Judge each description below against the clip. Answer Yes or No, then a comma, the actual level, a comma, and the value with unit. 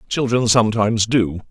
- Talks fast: No, slow, 120 wpm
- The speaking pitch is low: Yes, low, 110 Hz